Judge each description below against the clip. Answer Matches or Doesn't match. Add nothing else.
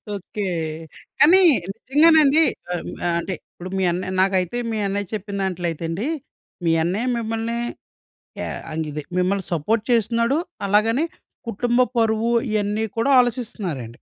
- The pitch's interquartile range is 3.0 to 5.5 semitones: Matches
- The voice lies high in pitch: Matches